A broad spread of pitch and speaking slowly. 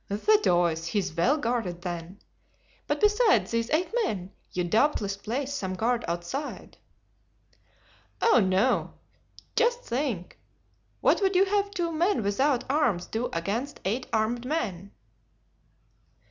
Yes: wide, 8.4 semitones; slow, 130 wpm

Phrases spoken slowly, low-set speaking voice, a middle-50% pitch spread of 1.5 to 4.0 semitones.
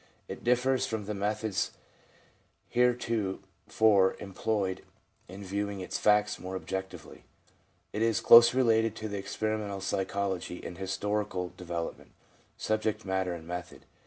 Yes: slow, 115 wpm; low, 100 Hz; narrow, 2.6 semitones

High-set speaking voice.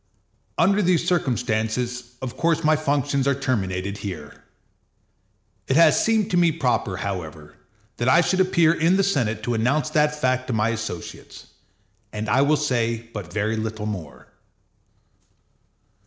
No: low, 125 Hz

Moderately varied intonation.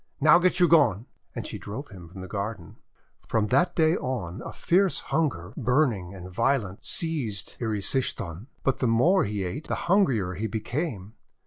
No: wide, 7.9 semitones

